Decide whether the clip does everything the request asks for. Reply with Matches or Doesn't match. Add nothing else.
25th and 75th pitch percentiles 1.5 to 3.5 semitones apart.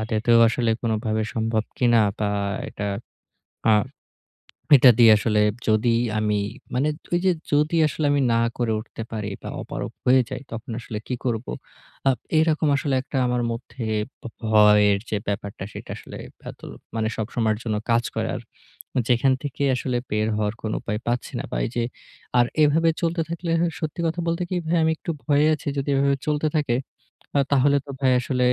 Doesn't match